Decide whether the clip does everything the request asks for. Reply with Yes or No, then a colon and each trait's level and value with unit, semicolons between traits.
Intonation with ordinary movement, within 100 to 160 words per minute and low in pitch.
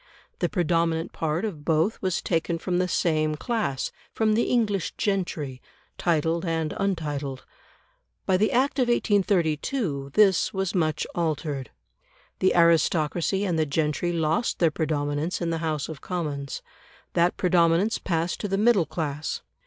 No: average, 3.7 semitones; average, 145 wpm; medium, 170 Hz